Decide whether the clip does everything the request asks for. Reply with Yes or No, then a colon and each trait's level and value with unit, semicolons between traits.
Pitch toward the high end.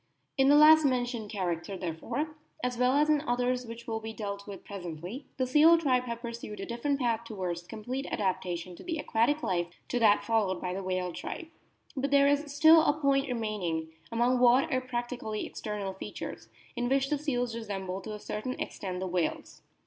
Yes: high, 235 Hz